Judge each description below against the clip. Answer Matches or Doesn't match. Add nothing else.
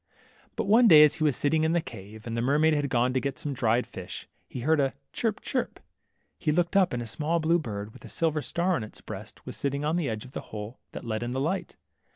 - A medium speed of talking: Doesn't match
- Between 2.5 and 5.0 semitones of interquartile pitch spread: Doesn't match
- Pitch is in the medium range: Matches